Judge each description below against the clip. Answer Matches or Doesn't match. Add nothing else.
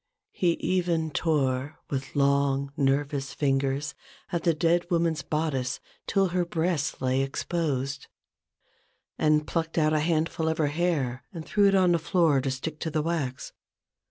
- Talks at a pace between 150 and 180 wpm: Matches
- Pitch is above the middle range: Doesn't match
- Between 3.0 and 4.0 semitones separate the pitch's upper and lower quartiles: Matches